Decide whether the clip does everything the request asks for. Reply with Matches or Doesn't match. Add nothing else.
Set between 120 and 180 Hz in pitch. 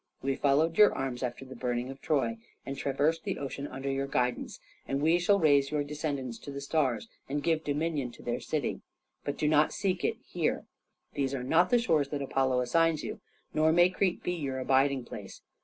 Matches